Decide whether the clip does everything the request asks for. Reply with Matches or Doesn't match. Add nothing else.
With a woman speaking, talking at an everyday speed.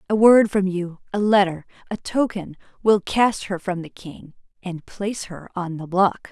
Matches